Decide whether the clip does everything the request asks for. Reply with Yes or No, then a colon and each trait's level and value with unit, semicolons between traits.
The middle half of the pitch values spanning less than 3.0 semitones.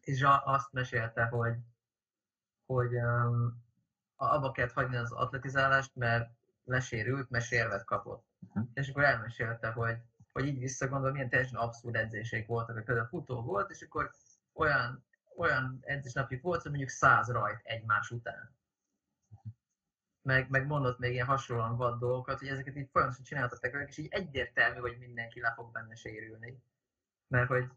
Yes: narrow, 2.5 semitones